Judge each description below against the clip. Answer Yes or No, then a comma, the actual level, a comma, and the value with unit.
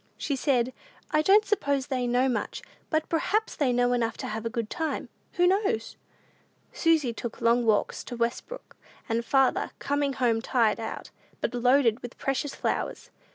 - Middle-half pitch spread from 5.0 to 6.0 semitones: No, average, 4.0 semitones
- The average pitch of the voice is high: Yes, very high, 255 Hz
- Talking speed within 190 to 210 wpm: No, average, 165 wpm